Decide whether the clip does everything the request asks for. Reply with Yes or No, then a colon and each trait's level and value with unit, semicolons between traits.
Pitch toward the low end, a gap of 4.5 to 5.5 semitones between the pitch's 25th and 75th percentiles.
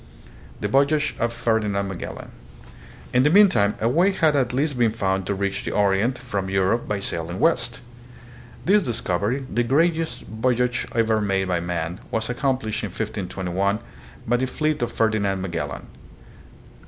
Yes: low, 110 Hz; average, 4.8 semitones